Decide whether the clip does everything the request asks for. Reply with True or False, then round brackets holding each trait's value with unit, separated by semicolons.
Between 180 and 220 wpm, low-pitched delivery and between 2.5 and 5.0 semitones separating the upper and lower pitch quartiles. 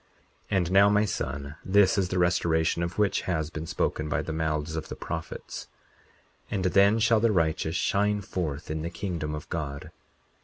True (190 wpm; 85 Hz; 3.9 semitones)